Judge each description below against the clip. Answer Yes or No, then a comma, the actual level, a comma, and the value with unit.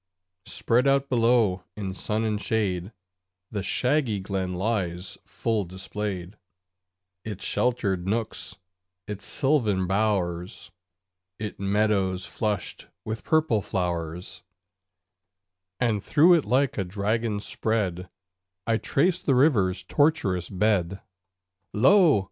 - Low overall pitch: Yes, low, 105 Hz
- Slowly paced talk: Yes, slow, 105 wpm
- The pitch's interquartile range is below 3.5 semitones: No, average, 3.8 semitones